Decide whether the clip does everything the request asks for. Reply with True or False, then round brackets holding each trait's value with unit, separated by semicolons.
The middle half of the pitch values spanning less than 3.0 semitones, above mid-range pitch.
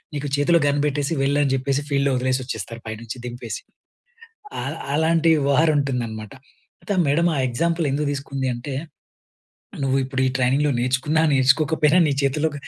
False (2.5 semitones; 140 Hz)